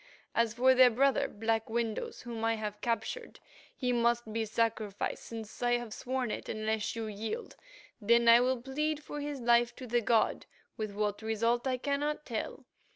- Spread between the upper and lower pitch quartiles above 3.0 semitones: No, narrow, 2.4 semitones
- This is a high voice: Yes, high, 235 Hz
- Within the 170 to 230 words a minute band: Yes, average, 175 wpm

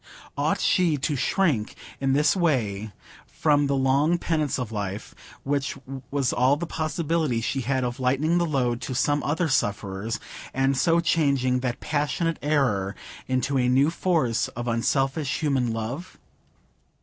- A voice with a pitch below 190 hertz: Yes, low, 135 Hz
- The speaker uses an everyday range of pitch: Yes, average, 3.9 semitones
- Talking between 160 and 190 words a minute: No, average, 150 wpm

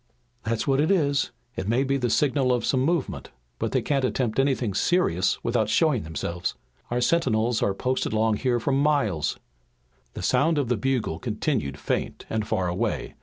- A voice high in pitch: No, low, 125 Hz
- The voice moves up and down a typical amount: Yes, average, 4.3 semitones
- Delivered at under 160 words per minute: No, average, 175 wpm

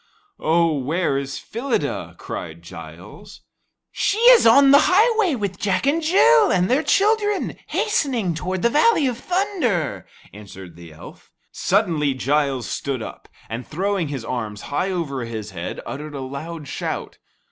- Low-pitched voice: No, medium, 175 Hz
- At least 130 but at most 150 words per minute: Yes, average, 145 wpm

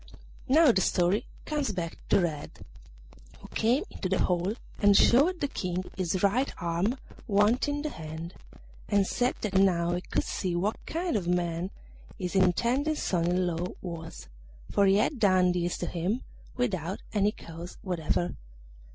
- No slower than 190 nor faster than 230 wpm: No, average, 160 wpm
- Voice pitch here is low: No, high, 190 Hz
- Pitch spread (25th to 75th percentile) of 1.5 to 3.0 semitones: No, average, 4.5 semitones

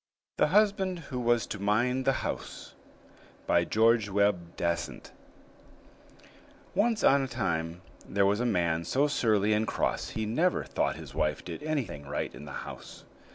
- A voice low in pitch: Yes, low, 110 Hz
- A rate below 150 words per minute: No, average, 155 wpm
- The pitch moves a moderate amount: No, wide, 7.6 semitones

